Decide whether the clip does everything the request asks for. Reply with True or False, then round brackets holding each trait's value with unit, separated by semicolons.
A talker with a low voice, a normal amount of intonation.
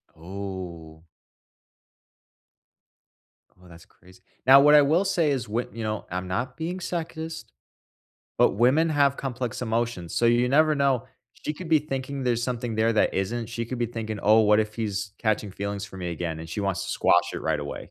False (115 Hz; 5.7 semitones)